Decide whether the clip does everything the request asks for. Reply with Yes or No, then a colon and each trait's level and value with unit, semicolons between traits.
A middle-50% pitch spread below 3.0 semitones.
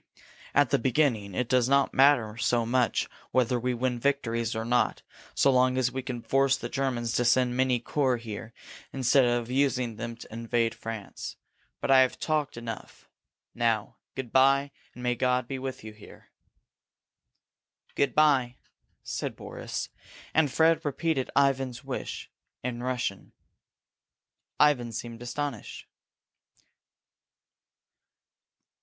Yes: narrow, 2.4 semitones